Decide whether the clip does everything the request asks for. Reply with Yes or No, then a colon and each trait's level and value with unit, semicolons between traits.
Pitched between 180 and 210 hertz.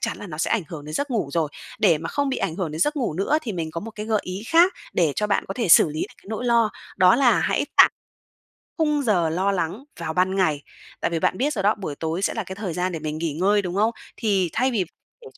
Yes: high, 195 Hz